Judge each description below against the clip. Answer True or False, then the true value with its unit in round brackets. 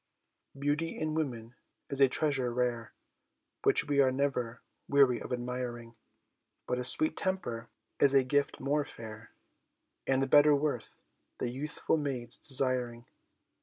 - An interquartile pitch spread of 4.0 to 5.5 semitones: False (2.9 semitones)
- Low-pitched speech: True (130 Hz)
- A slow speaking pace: True (130 wpm)